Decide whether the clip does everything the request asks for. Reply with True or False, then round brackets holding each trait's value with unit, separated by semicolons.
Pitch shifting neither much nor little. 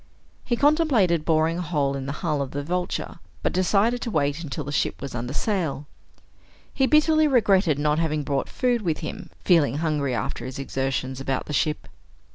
False (5.8 semitones)